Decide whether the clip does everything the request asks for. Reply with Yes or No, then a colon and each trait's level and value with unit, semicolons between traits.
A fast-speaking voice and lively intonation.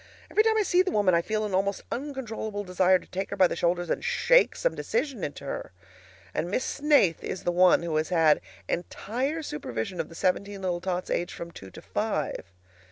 Yes: fast, 210 wpm; wide, 7.2 semitones